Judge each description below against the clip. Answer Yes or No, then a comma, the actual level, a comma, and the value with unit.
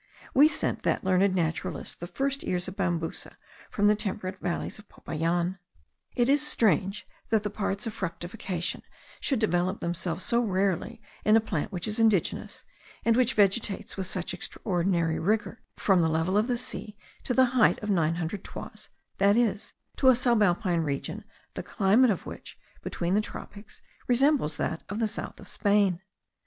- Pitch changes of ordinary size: Yes, average, 4.1 semitones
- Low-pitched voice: No, high, 200 Hz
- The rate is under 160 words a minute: No, average, 170 wpm